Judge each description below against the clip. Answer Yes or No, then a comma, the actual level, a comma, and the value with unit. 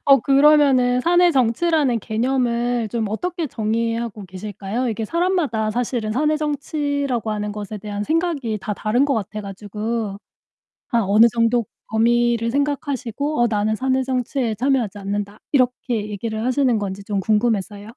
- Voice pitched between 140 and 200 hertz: No, high, 235 Hz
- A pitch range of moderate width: Yes, average, 4.1 semitones